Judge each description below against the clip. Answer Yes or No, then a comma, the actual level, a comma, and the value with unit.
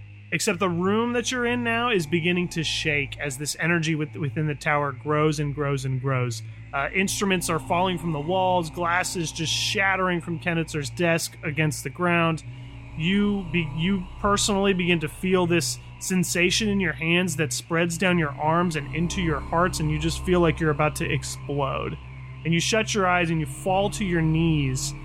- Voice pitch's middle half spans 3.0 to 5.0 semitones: Yes, average, 3.8 semitones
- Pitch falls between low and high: Yes, medium, 165 Hz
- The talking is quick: No, average, 190 wpm